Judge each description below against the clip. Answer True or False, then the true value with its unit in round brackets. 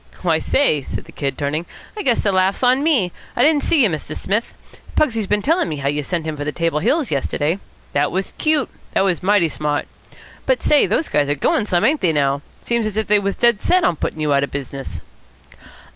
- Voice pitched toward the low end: False (185 Hz)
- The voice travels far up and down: True (8.1 semitones)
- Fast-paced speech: True (230 wpm)